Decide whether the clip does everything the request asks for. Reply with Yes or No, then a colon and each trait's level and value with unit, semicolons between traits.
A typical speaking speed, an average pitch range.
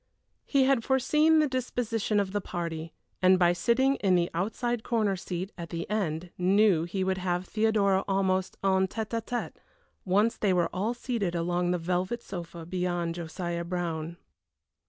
Yes: average, 165 wpm; average, 4.1 semitones